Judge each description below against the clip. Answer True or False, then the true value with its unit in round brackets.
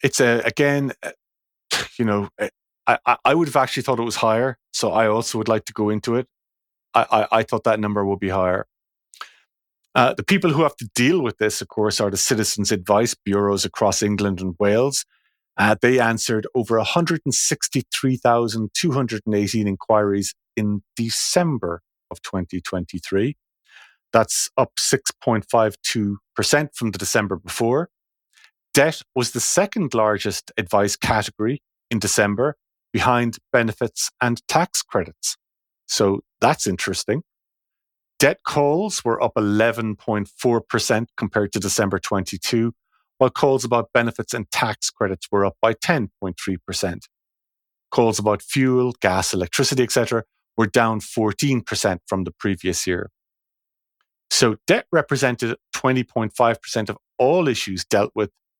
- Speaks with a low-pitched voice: True (110 Hz)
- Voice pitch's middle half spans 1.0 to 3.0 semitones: False (3.4 semitones)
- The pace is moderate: False (130 wpm)